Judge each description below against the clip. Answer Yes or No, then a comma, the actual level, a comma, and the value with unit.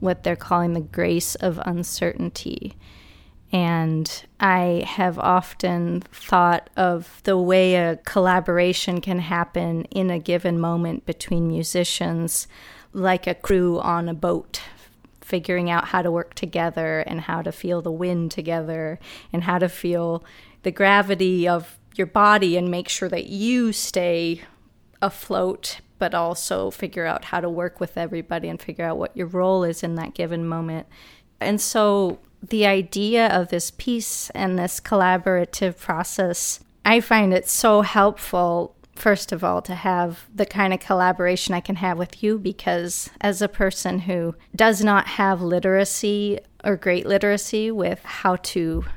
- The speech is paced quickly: No, average, 155 wpm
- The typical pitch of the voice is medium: Yes, medium, 180 Hz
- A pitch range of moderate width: No, narrow, 2.1 semitones